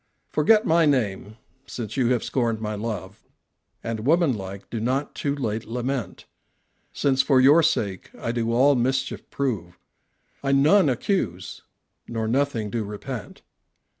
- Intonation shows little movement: No, average, 4.2 semitones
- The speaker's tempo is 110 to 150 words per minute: Yes, average, 140 wpm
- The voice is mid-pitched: No, low, 120 Hz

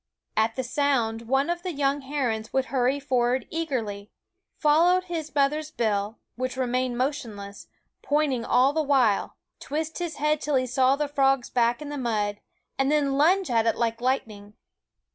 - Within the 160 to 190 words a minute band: Yes, average, 170 wpm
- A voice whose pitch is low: No, very high, 265 Hz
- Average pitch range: Yes, average, 3.9 semitones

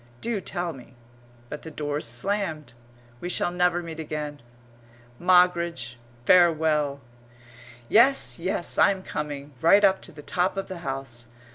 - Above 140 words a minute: No, slow, 135 wpm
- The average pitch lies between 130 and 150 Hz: No, medium, 165 Hz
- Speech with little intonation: No, average, 3.7 semitones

